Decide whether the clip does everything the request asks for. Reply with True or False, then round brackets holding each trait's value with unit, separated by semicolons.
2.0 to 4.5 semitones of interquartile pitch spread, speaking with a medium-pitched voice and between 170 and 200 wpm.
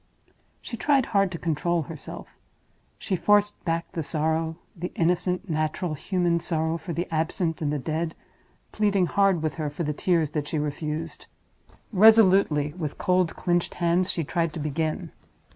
False (2.7 semitones; 170 Hz; 150 wpm)